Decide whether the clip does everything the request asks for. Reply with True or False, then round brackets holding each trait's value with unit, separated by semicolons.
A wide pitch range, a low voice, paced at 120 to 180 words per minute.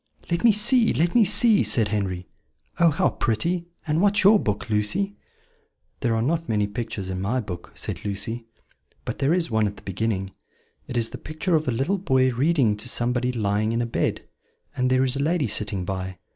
False (8.0 semitones; 125 Hz; 200 wpm)